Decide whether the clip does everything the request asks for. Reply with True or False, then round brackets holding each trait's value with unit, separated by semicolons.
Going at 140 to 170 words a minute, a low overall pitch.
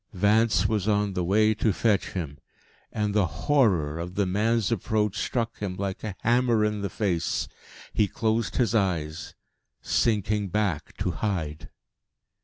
True (150 wpm; 105 Hz)